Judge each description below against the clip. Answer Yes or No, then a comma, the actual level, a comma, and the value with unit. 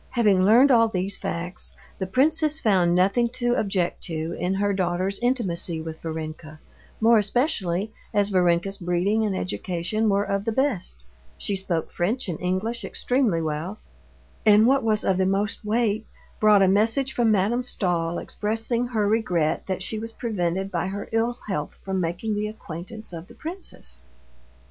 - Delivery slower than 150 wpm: No, average, 160 wpm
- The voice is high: Yes, high, 200 Hz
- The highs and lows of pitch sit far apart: No, average, 4.2 semitones